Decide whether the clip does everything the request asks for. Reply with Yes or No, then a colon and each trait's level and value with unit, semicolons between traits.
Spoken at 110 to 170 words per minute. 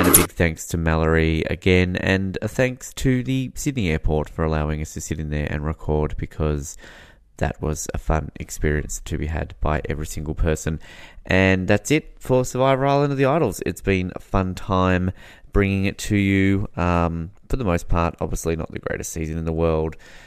No: average, 200 wpm